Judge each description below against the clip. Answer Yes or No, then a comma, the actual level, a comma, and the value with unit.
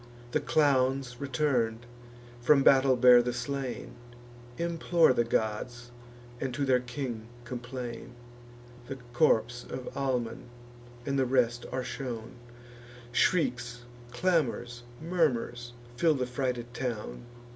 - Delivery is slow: Yes, slow, 110 wpm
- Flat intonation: Yes, narrow, 2.2 semitones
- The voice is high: No, low, 125 Hz